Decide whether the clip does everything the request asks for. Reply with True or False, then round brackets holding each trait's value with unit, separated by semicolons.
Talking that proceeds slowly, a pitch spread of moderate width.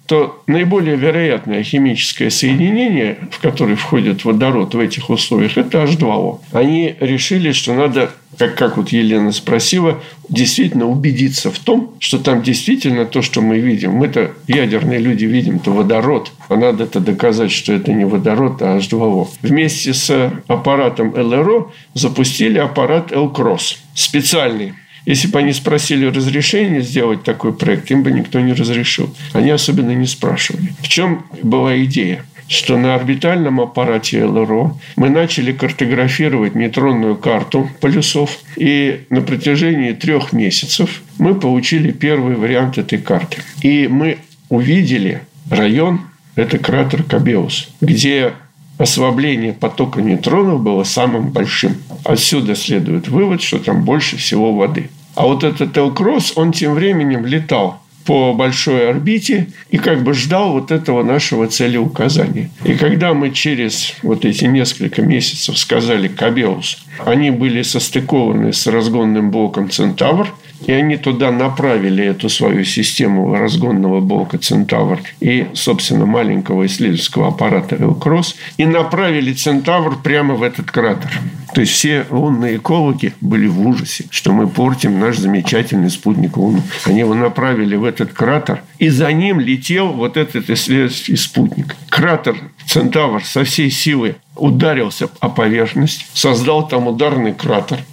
False (135 wpm; 3.9 semitones)